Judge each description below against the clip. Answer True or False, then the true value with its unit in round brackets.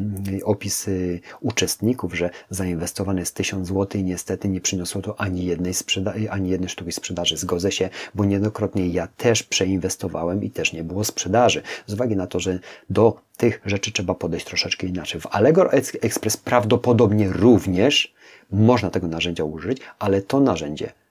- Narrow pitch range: True (2.3 semitones)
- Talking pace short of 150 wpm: False (155 wpm)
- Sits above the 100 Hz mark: False (95 Hz)